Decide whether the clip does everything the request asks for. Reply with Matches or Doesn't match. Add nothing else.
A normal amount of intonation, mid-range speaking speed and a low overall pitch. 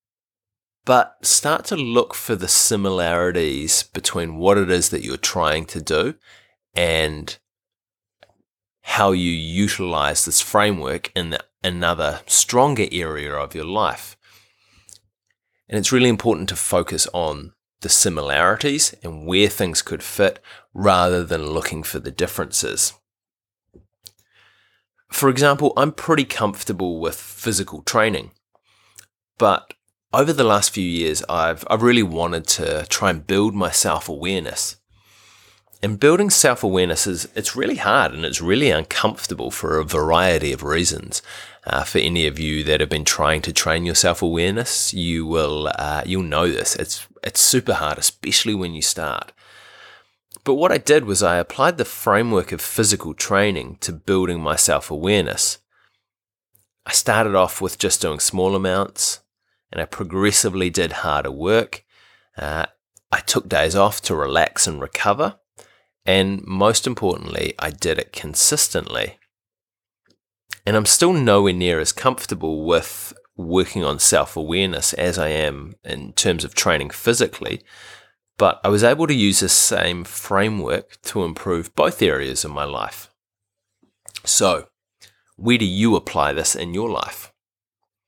Matches